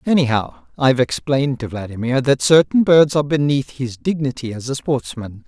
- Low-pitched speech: Yes, low, 130 Hz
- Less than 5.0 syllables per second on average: No, 5.4 syllables/s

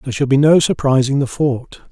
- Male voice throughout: Yes, male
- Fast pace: Yes, fast, 220 wpm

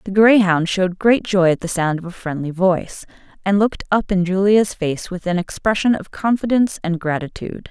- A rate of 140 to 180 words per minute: No, average, 195 wpm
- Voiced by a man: No, female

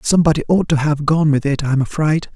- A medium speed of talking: No, fast, 230 wpm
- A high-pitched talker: No, medium, 150 Hz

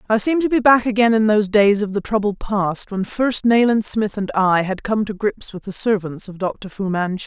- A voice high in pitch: Yes, high, 210 Hz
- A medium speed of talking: No, fast, 250 wpm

